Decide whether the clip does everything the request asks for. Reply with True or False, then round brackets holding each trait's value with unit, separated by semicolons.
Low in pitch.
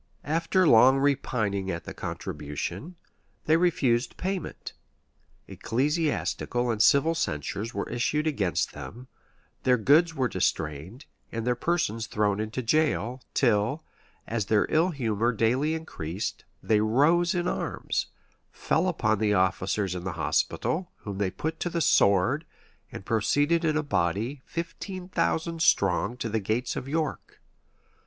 True (125 Hz)